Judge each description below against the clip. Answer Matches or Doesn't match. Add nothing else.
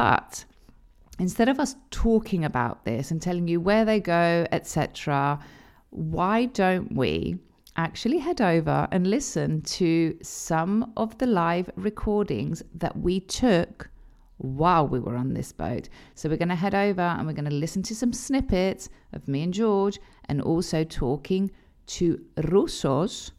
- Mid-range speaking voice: Matches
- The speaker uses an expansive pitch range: Doesn't match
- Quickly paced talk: Doesn't match